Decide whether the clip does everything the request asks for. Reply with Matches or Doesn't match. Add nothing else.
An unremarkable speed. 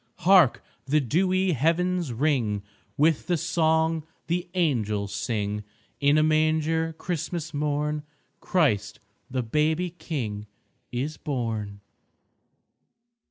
Doesn't match